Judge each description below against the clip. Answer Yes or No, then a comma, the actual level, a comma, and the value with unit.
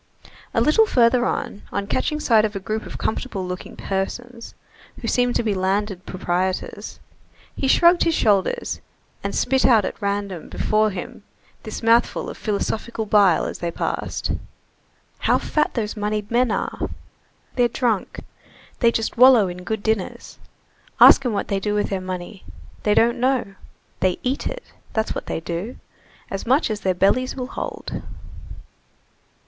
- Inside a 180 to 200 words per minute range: No, average, 160 wpm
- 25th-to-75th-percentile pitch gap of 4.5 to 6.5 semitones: No, average, 3.8 semitones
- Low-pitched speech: No, high, 215 Hz